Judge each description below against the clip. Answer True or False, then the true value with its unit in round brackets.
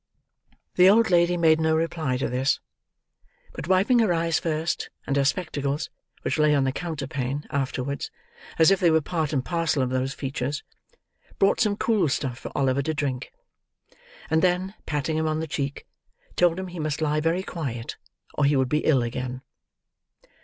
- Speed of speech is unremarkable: True (175 wpm)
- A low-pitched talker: False (155 Hz)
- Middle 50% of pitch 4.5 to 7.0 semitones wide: False (3.8 semitones)